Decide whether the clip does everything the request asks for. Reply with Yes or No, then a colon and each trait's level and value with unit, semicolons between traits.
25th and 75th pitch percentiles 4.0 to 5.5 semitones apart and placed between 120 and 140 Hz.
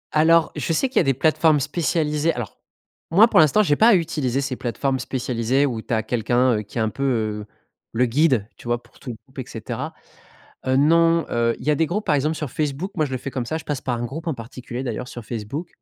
Yes: average, 4.7 semitones; low, 135 Hz